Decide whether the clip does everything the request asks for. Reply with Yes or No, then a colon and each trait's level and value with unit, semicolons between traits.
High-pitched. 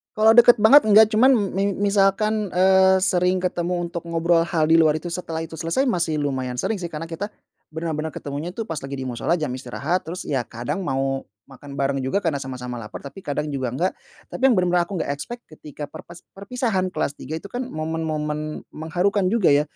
No: medium, 165 Hz